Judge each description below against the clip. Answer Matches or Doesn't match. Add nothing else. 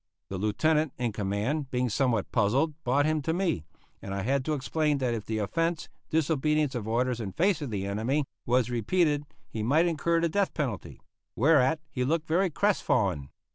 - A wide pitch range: Matches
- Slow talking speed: Doesn't match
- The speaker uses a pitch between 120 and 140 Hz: Matches